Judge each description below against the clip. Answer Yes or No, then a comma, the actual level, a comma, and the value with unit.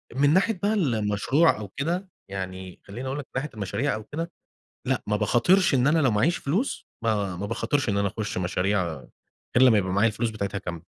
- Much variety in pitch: Yes, wide, 6.6 semitones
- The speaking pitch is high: No, low, 110 Hz